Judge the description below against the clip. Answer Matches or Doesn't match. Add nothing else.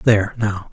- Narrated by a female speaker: Doesn't match